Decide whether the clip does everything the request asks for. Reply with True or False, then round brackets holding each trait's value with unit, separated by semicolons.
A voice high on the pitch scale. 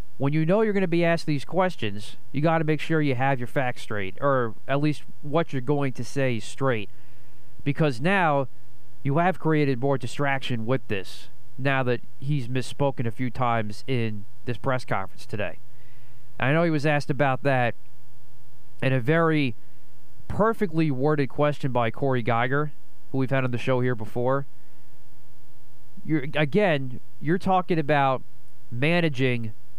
False (135 Hz)